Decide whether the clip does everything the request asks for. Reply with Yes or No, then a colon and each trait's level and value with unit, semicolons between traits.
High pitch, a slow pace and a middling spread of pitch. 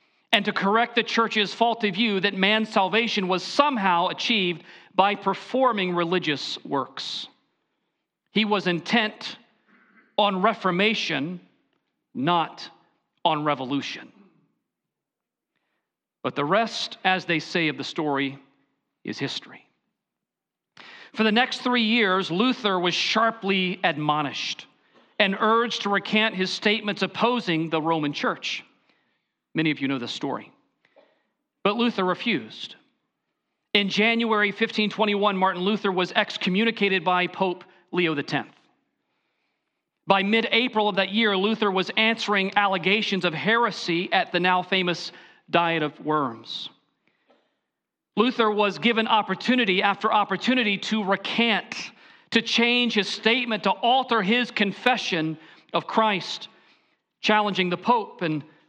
Yes: high, 200 Hz; slow, 120 wpm; average, 3.7 semitones